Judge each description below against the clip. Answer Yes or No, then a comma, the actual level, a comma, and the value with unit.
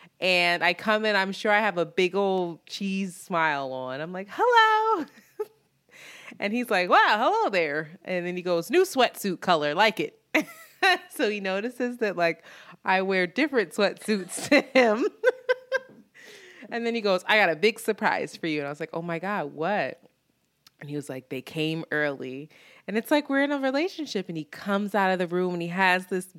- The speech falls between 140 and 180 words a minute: No, average, 200 wpm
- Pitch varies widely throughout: Yes, wide, 6.3 semitones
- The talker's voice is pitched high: Yes, high, 195 Hz